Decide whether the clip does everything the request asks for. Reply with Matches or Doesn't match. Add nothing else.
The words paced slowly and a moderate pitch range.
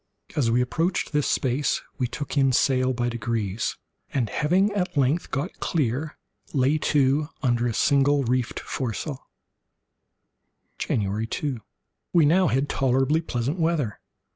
Matches